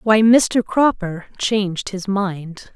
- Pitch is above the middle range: Yes, high, 200 Hz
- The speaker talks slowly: Yes, slow, 130 wpm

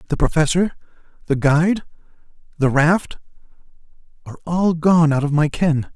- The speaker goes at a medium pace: No, slow, 120 wpm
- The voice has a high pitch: No, medium, 160 Hz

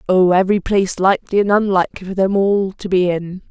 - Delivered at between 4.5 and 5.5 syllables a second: No, 6.1 syllables/s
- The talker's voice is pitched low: No, high, 190 Hz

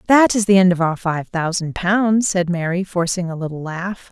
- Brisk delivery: Yes, fast, 220 wpm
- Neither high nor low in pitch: Yes, medium, 180 Hz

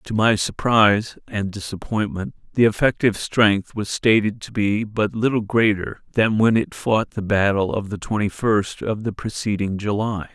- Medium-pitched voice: No, low, 105 Hz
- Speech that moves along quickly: No, average, 170 wpm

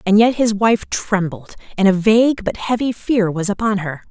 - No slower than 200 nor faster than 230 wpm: Yes, fast, 205 wpm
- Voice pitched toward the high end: Yes, high, 205 Hz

